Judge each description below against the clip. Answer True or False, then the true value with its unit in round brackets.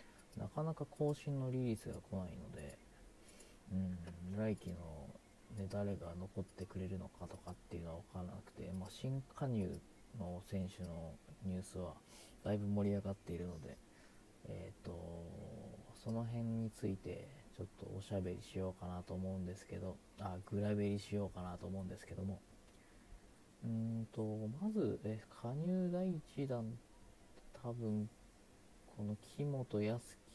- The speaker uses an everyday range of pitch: True (3.5 semitones)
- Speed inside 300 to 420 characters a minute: False (285 characters per minute)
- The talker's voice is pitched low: True (100 Hz)